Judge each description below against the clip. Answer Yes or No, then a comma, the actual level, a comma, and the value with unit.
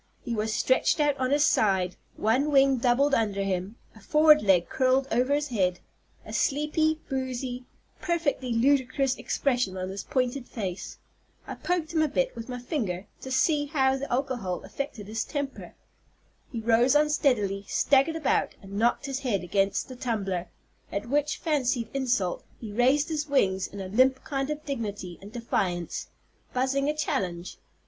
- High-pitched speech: Yes, very high, 255 Hz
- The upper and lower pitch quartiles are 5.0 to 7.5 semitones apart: Yes, wide, 5.5 semitones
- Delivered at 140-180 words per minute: Yes, average, 165 wpm